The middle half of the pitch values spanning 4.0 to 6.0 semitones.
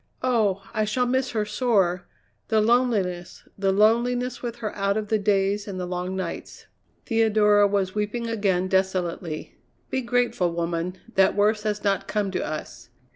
No: average, 3.3 semitones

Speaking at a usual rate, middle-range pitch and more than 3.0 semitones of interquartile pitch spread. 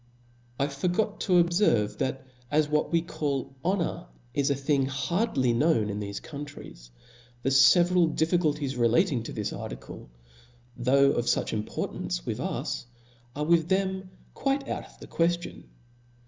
Yes: average, 150 wpm; medium, 145 Hz; average, 5.2 semitones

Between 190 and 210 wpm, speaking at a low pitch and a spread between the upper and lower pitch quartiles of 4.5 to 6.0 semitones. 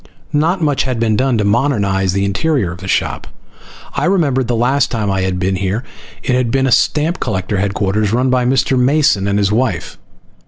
Yes: fast, 205 wpm; low, 115 Hz; average, 5.2 semitones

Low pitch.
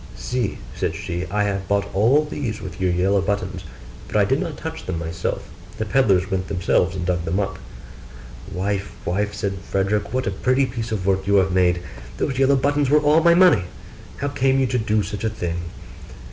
Yes: low, 100 Hz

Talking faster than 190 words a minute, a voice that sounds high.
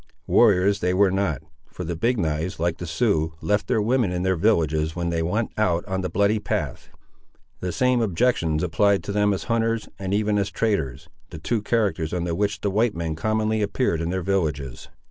No: average, 200 wpm; very low, 95 Hz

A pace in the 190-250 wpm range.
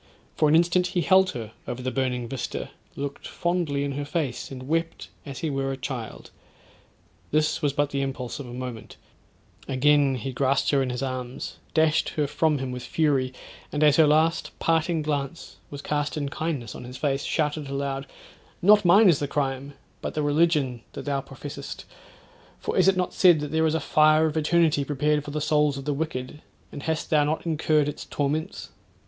Yes: average, 195 wpm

